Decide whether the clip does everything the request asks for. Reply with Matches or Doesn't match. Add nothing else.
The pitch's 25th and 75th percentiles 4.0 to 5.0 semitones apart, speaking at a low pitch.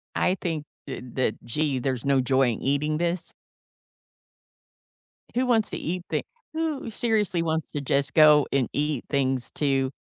Doesn't match